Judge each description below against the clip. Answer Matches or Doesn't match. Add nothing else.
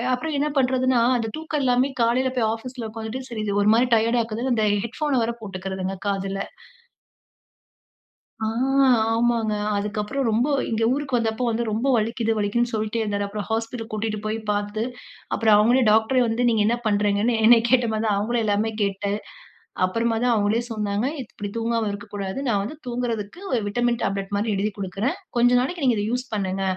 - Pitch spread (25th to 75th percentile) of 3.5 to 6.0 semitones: Doesn't match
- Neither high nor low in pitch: Doesn't match